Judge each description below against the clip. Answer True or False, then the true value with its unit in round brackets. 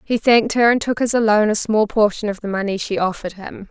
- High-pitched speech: True (215 Hz)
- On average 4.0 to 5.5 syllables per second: False (6.1 syllables/s)